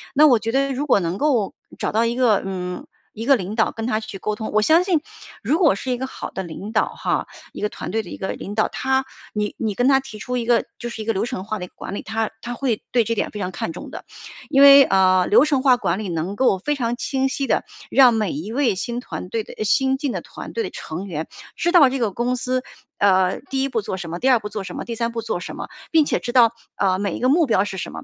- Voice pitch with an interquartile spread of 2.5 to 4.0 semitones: No, average, 4.9 semitones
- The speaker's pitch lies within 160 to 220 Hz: No, high, 230 Hz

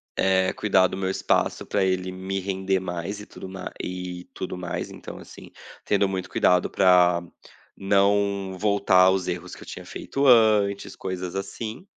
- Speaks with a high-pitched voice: No, very low, 95 Hz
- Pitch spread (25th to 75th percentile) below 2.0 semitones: Yes, narrow, 1.5 semitones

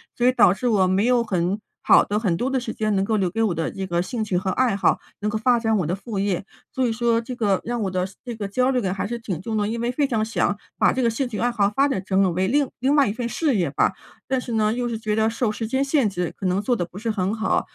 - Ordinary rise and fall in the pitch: Yes, average, 3.8 semitones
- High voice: Yes, high, 220 Hz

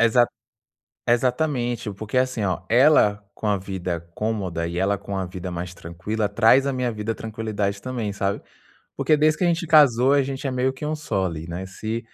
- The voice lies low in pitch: Yes, low, 110 Hz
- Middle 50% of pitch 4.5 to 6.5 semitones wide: Yes, average, 4.8 semitones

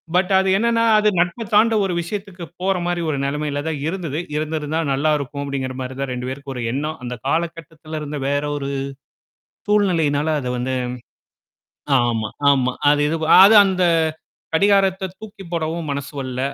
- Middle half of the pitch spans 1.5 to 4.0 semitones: No, average, 4.8 semitones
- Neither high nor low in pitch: Yes, medium, 155 Hz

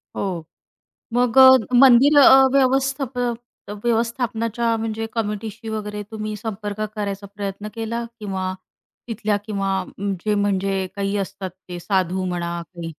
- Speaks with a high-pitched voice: Yes, high, 210 Hz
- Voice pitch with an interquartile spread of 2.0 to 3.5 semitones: Yes, average, 2.9 semitones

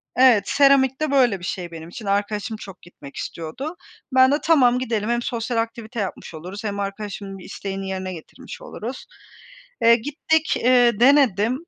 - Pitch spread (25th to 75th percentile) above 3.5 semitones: Yes, average, 4.8 semitones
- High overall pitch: Yes, high, 225 Hz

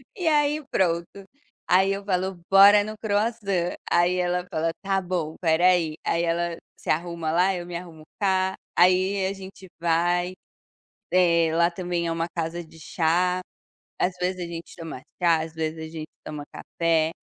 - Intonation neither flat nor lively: No, narrow, 2.2 semitones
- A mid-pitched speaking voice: Yes, medium, 175 Hz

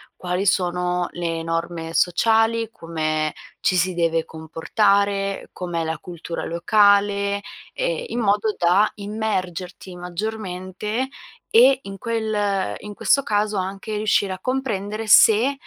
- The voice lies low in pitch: No, high, 195 Hz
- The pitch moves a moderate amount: Yes, average, 3.5 semitones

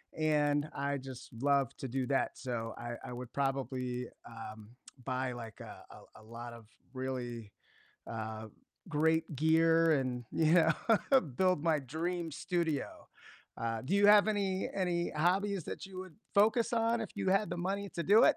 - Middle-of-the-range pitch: Yes, medium, 150 Hz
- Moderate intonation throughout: No, wide, 6.5 semitones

